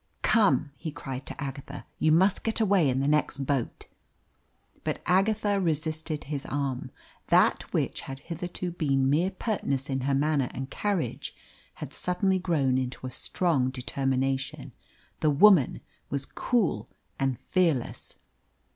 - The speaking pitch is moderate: Yes, medium, 145 Hz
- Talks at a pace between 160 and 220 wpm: No, average, 140 wpm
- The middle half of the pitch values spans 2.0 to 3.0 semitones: No, average, 5.0 semitones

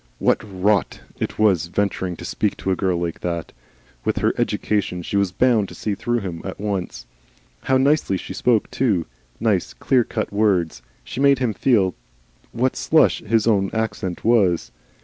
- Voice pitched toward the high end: No, low, 100 Hz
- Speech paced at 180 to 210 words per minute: No, average, 170 wpm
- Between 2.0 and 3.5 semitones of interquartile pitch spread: No, average, 4.0 semitones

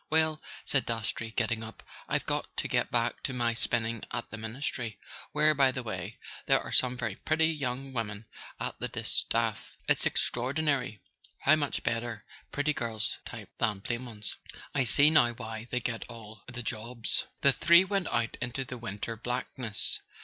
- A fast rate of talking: No, average, 170 wpm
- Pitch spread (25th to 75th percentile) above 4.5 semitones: No, average, 3.3 semitones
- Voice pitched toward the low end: Yes, low, 120 Hz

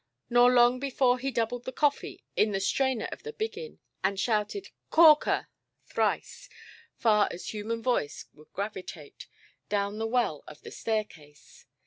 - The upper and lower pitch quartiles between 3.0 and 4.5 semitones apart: Yes, average, 4.1 semitones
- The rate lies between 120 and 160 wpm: Yes, average, 145 wpm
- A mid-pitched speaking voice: No, high, 230 Hz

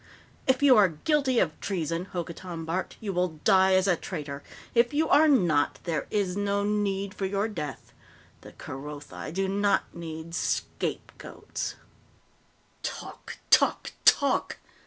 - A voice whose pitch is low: No, high, 190 Hz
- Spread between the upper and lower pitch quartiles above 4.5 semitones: No, average, 3.8 semitones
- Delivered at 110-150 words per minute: Yes, slow, 135 wpm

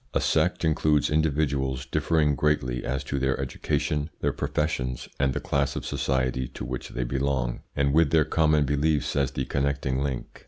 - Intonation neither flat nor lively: No, narrow, 2.3 semitones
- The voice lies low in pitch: Yes, very low, 70 Hz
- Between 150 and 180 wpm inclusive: Yes, average, 170 wpm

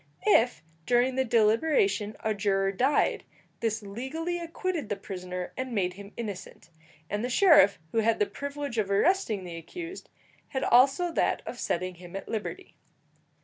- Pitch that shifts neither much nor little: No, wide, 6.1 semitones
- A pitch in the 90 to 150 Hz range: No, high, 225 Hz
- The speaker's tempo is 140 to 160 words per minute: Yes, average, 155 wpm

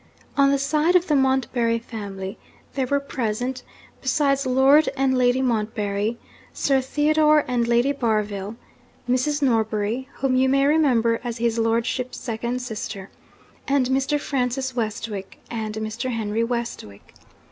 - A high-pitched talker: Yes, very high, 250 Hz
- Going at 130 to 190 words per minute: Yes, slow, 135 wpm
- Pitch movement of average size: Yes, average, 3.3 semitones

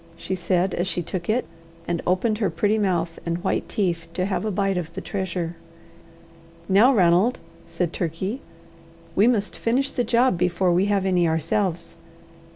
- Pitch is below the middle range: No, medium, 185 Hz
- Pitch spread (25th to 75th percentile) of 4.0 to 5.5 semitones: No, average, 3.2 semitones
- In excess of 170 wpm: No, average, 165 wpm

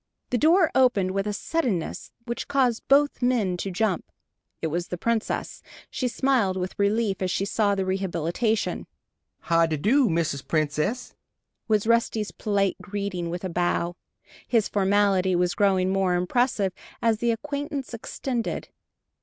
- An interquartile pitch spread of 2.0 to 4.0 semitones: No, average, 4.6 semitones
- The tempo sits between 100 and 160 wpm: Yes, average, 145 wpm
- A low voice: No, high, 200 Hz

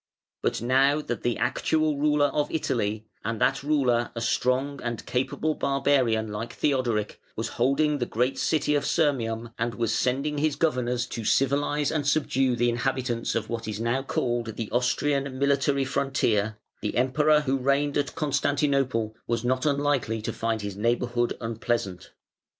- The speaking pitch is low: Yes, low, 130 Hz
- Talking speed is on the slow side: No, average, 155 wpm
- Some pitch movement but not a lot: Yes, average, 3.5 semitones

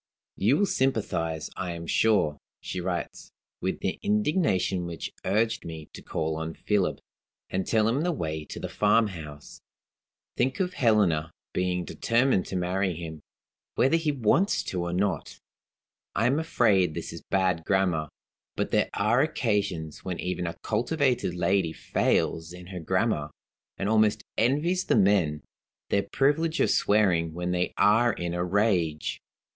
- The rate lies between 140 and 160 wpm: Yes, average, 150 wpm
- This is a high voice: No, very low, 95 Hz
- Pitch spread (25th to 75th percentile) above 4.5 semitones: Yes, average, 5.1 semitones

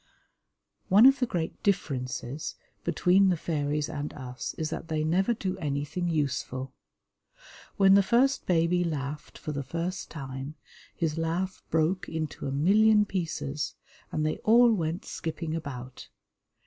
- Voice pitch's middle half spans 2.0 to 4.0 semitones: No, average, 4.5 semitones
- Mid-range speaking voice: Yes, medium, 165 Hz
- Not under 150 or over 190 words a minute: No, average, 140 wpm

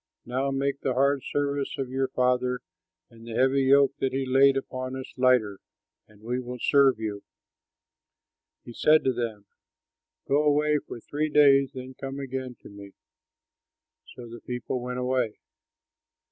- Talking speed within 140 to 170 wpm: Yes, average, 155 wpm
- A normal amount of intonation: No, narrow, 1.9 semitones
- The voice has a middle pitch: No, low, 130 Hz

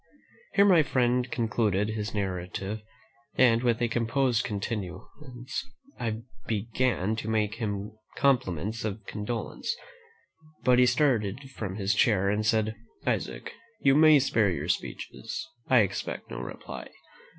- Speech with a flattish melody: No, average, 3.4 semitones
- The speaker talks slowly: Yes, slow, 130 wpm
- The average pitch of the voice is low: Yes, low, 110 Hz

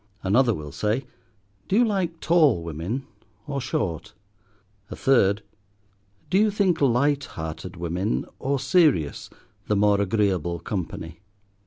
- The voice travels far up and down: Yes, wide, 8.5 semitones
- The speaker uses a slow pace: Yes, slow, 125 wpm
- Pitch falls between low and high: No, low, 110 Hz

